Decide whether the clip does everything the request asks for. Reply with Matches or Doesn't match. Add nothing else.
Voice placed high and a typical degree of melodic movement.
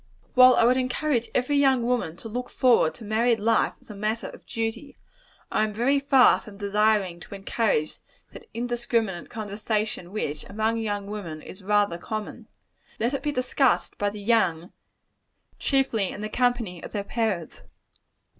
Matches